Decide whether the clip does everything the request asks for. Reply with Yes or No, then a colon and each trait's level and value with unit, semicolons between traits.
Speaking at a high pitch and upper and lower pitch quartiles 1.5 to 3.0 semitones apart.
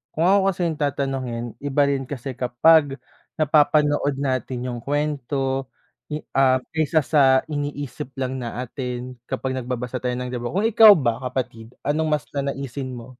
No: low, 135 Hz; narrow, 2.6 semitones